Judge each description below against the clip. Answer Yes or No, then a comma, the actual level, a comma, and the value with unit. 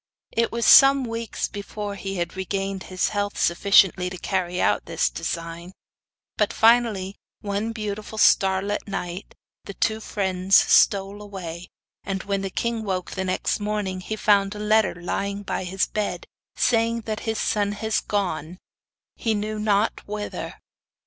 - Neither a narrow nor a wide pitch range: No, narrow, 2.2 semitones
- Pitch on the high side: Yes, high, 200 Hz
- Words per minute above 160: No, average, 150 wpm